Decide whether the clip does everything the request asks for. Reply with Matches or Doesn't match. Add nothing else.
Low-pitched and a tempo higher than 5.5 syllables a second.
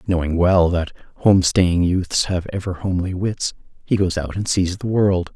Doesn't match